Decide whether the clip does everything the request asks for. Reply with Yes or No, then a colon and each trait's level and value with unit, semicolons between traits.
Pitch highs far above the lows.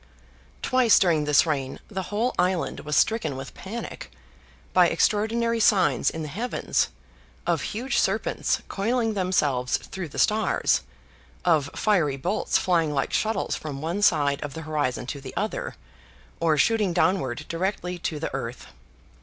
Yes: wide, 6.3 semitones